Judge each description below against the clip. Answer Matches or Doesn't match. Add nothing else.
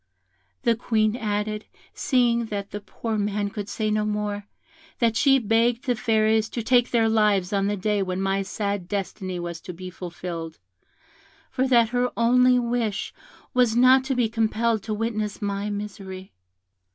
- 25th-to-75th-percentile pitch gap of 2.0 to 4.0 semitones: Matches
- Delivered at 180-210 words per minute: Doesn't match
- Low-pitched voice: Doesn't match